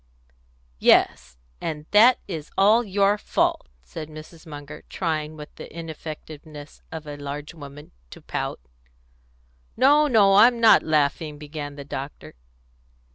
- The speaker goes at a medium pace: No, slow, 130 wpm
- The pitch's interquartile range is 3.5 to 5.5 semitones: Yes, average, 5.2 semitones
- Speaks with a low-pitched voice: No, medium, 155 Hz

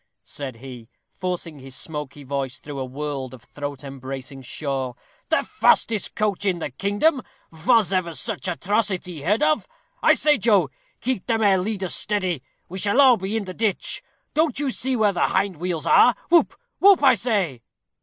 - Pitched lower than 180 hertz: No, medium, 185 Hz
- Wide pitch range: Yes, wide, 7.6 semitones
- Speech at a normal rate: Yes, average, 175 wpm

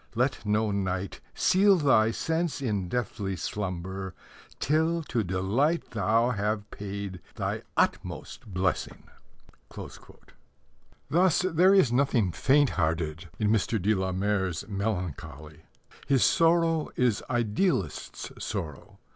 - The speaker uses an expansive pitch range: Yes, wide, 6.7 semitones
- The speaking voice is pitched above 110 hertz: No, low, 105 Hz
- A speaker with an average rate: No, slow, 110 wpm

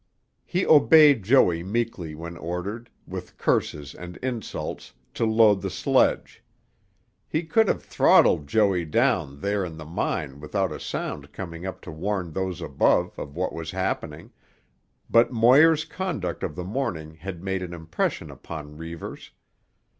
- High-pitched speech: No, very low, 95 Hz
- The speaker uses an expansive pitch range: Yes, wide, 5.8 semitones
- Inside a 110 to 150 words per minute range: Yes, average, 145 wpm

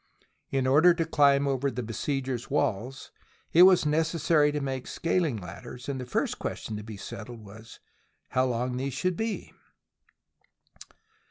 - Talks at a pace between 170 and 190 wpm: No, average, 150 wpm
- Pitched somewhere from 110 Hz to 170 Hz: Yes, low, 135 Hz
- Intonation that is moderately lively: Yes, average, 3.8 semitones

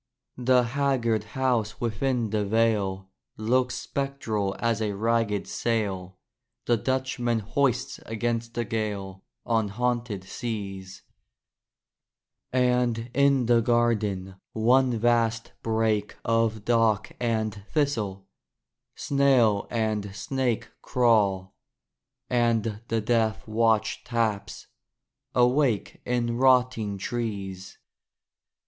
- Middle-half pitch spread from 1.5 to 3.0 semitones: Yes, narrow, 2.6 semitones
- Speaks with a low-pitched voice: Yes, low, 115 Hz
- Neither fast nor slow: No, slow, 95 wpm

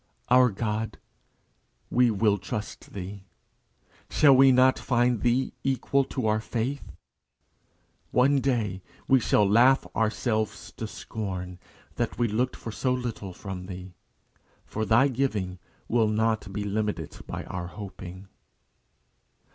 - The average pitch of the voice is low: Yes, low, 110 Hz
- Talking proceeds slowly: Yes, slow, 125 wpm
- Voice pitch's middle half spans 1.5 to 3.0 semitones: No, average, 3.9 semitones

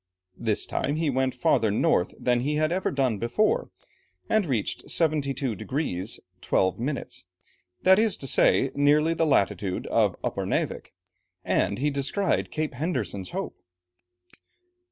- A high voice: No, medium, 140 Hz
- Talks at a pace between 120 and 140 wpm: Yes, slow, 135 wpm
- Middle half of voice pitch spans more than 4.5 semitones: Yes, average, 5.0 semitones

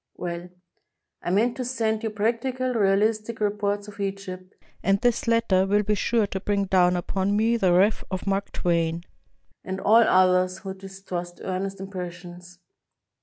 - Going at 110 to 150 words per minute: No, average, 160 wpm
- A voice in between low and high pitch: No, high, 195 Hz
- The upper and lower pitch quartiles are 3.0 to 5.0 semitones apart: No, narrow, 2.6 semitones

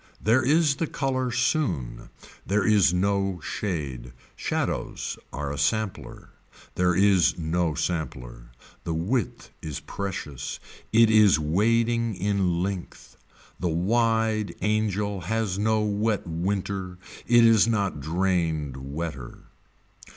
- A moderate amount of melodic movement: Yes, average, 4.8 semitones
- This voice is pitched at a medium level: No, very low, 95 Hz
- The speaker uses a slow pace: Yes, slow, 115 wpm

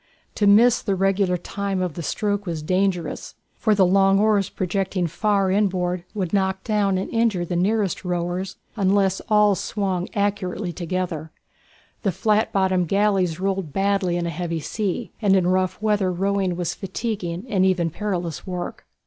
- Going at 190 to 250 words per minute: No, average, 160 wpm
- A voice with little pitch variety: Yes, narrow, 2.1 semitones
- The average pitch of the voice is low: No, high, 190 Hz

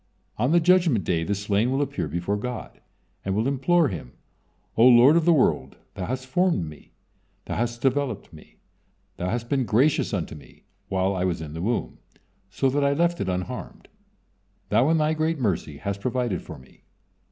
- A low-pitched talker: Yes, low, 120 Hz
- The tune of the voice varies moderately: No, wide, 7.3 semitones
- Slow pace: No, average, 185 wpm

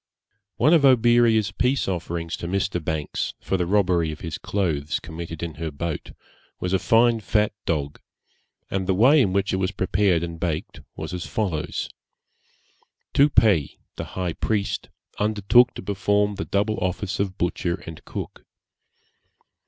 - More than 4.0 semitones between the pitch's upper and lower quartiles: No, average, 3.7 semitones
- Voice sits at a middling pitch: No, very low, 95 Hz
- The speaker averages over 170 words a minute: No, average, 150 wpm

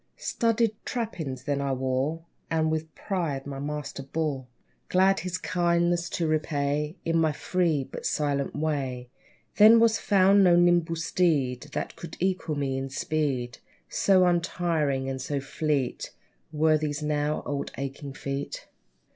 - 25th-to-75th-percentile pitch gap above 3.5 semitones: Yes, average, 3.9 semitones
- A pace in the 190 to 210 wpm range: No, average, 140 wpm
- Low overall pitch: No, medium, 155 Hz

